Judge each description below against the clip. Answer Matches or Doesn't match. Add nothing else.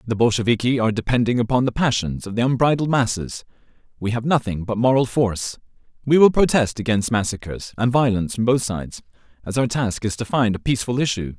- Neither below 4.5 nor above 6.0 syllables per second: Doesn't match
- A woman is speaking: Doesn't match